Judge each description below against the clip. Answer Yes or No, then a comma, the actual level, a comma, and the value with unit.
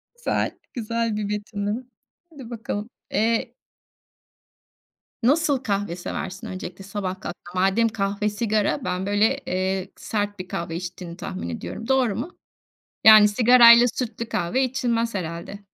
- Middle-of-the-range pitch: No, high, 210 Hz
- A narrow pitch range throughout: No, average, 3.5 semitones